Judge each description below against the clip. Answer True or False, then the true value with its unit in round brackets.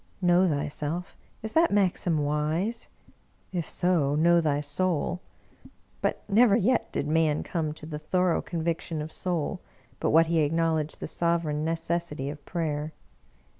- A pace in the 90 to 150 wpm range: True (140 wpm)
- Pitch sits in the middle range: True (165 Hz)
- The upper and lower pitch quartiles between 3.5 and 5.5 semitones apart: False (2.8 semitones)